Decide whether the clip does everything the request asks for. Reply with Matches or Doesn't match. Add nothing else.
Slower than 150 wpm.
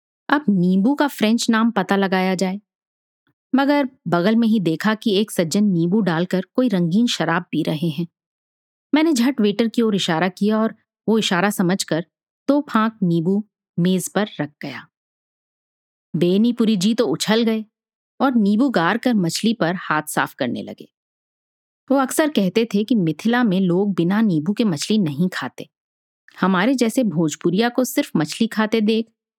Doesn't match